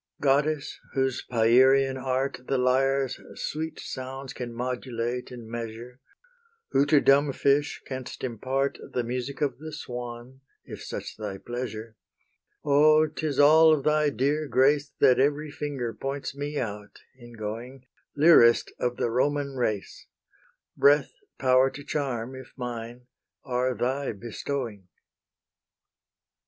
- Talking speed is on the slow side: Yes, slow, 125 wpm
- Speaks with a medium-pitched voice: No, low, 130 Hz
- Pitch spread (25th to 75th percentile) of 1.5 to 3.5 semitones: Yes, average, 2.8 semitones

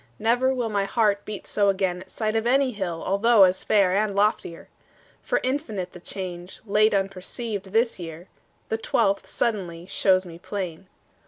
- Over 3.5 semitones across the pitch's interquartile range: No, average, 3.1 semitones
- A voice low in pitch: No, high, 200 Hz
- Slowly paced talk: No, average, 165 wpm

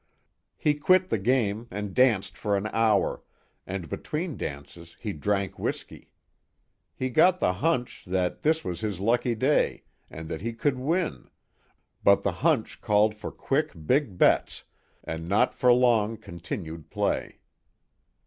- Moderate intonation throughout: No, wide, 5.7 semitones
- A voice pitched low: Yes, low, 110 Hz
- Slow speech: No, average, 145 wpm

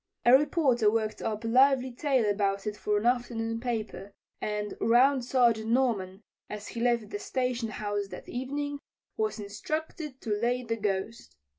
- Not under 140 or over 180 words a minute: Yes, average, 160 wpm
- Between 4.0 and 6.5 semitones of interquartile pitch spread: No, average, 3.4 semitones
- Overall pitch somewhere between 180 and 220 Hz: No, high, 235 Hz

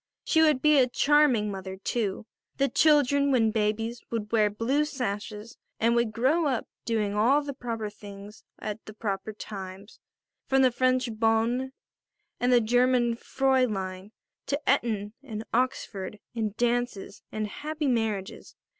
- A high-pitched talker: Yes, high, 230 Hz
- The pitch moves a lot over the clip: No, average, 3.7 semitones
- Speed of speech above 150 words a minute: No, average, 145 wpm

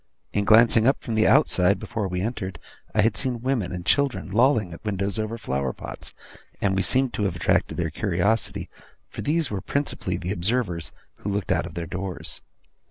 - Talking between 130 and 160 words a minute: No, average, 195 wpm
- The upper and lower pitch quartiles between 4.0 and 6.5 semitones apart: Yes, average, 4.3 semitones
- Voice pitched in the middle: No, low, 100 Hz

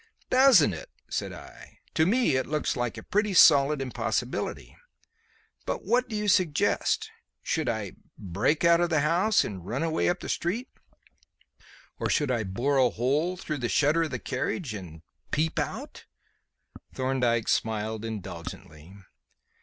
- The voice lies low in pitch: No, medium, 145 Hz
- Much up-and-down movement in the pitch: Yes, wide, 7.6 semitones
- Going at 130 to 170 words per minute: Yes, average, 150 wpm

